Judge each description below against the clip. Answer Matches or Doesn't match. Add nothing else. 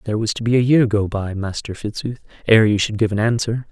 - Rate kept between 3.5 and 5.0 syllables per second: Doesn't match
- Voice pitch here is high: Doesn't match